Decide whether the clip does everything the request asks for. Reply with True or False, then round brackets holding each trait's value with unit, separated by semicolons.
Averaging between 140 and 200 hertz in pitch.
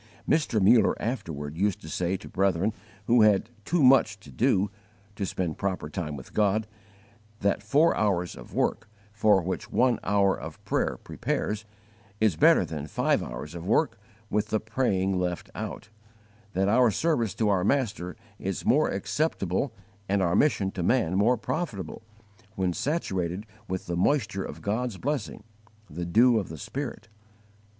False (100 Hz)